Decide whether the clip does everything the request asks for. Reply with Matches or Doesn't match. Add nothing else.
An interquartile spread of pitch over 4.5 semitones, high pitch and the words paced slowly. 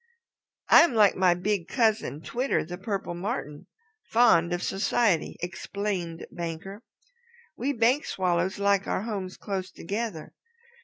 Doesn't match